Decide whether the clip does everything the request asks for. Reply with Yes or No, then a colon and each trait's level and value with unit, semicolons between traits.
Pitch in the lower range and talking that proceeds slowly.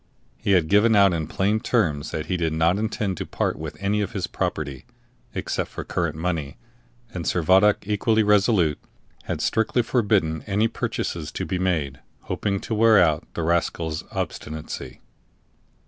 No: very low, 95 Hz; average, 160 wpm